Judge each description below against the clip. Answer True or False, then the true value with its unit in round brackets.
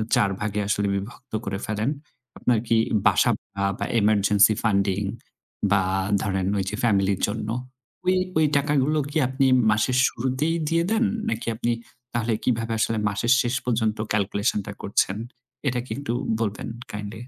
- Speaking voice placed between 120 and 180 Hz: False (110 Hz)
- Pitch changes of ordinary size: True (3.7 semitones)